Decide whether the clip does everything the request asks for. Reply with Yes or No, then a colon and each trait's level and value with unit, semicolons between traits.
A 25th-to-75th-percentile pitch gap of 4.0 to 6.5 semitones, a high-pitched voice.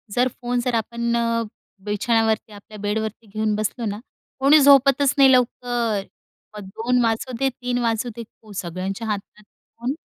No: average, 2.8 semitones; high, 230 Hz